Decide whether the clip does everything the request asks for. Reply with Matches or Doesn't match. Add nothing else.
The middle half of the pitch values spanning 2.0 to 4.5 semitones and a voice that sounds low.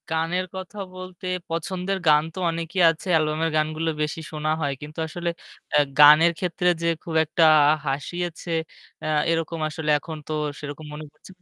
Doesn't match